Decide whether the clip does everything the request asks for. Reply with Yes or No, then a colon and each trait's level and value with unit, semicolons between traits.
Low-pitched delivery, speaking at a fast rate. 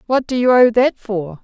No: high, 230 Hz; fast, 250 wpm